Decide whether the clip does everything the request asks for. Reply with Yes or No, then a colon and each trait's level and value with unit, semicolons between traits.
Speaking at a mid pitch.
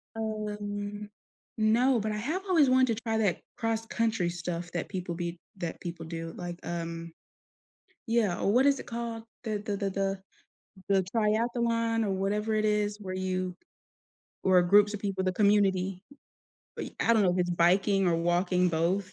No: high, 200 Hz